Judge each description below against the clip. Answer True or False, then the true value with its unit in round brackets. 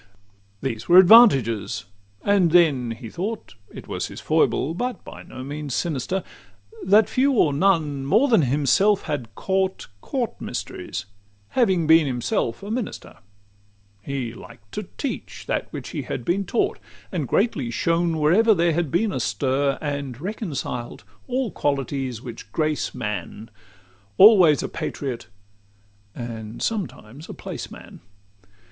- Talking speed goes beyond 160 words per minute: False (140 wpm)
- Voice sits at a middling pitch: True (155 Hz)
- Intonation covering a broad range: True (7.1 semitones)